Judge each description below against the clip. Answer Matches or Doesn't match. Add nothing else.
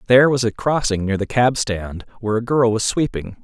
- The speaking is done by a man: Matches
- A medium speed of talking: Doesn't match